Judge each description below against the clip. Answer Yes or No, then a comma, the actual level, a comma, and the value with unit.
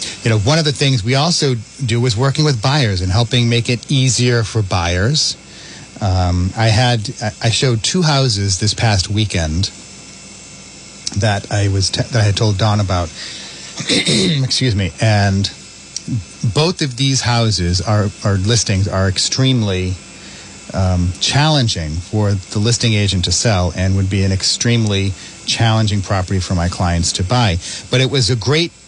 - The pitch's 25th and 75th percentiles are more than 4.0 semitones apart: Yes, average, 4.5 semitones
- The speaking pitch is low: Yes, low, 105 Hz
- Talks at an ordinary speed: Yes, average, 160 wpm